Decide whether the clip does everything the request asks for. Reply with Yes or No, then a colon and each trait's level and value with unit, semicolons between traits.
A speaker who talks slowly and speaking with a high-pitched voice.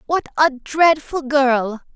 Yes: slow, 125 wpm; very high, 280 Hz